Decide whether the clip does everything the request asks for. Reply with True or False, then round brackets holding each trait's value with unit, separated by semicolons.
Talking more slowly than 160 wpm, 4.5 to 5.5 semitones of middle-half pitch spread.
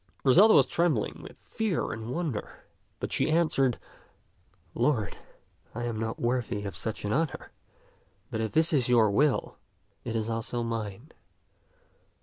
True (145 wpm; 5.2 semitones)